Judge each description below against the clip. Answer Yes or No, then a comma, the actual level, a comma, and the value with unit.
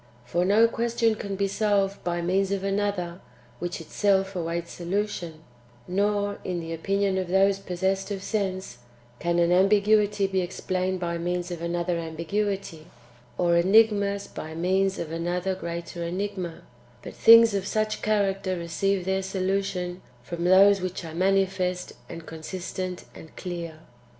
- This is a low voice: No, medium, 185 Hz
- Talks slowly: No, average, 145 wpm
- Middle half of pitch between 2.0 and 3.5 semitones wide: Yes, narrow, 2.4 semitones